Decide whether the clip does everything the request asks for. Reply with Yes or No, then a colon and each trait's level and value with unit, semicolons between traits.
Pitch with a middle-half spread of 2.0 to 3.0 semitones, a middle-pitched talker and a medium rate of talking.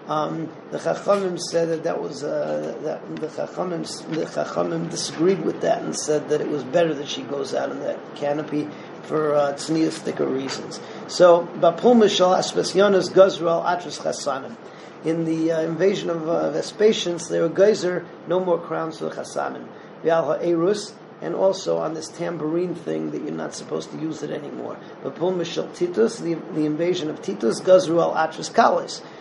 Yes: narrow, 2.5 semitones; medium, 170 Hz; average, 175 wpm